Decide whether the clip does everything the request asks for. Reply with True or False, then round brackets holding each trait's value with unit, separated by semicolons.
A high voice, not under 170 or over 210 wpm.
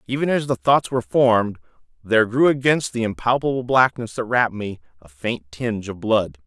False (115 Hz; 185 wpm)